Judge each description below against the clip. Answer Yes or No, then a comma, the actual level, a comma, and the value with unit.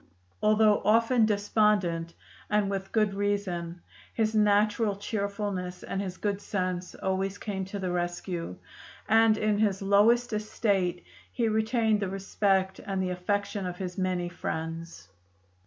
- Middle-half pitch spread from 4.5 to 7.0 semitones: No, narrow, 2.6 semitones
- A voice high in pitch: Yes, high, 200 Hz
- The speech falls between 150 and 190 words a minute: No, slow, 135 wpm